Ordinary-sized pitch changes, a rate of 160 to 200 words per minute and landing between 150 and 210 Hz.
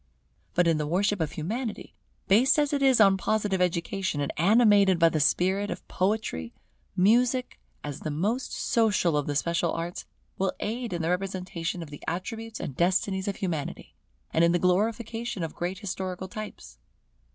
Yes: average, 4.1 semitones; average, 170 wpm; high, 190 Hz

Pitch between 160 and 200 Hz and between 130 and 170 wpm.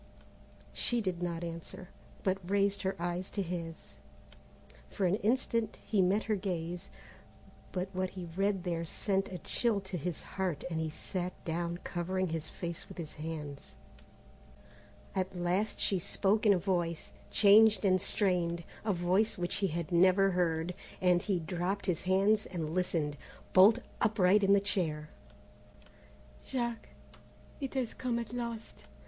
Yes: medium, 185 Hz; average, 150 wpm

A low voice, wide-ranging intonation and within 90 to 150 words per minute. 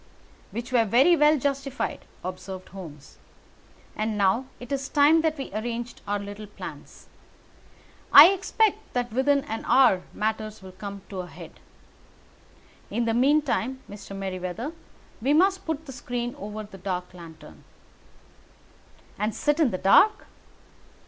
No: high, 230 Hz; wide, 6.0 semitones; average, 140 wpm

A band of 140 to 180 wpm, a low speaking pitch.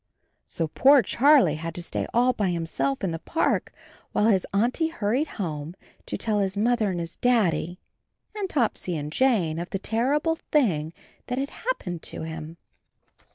No: average, 170 wpm; high, 200 Hz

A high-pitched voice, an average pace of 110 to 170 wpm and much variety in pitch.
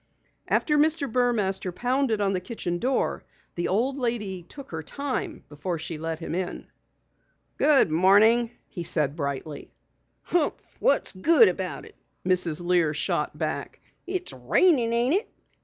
Yes: high, 200 Hz; average, 140 wpm; wide, 7.1 semitones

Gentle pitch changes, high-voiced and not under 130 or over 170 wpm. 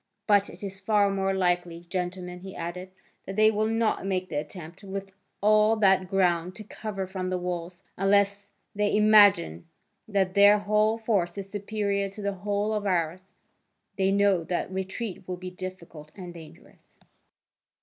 Yes: narrow, 2.2 semitones; high, 195 Hz; average, 160 wpm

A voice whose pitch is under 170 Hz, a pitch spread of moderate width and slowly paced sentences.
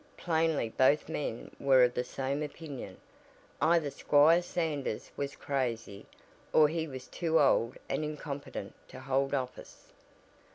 Yes: medium, 140 Hz; average, 3.3 semitones; slow, 130 wpm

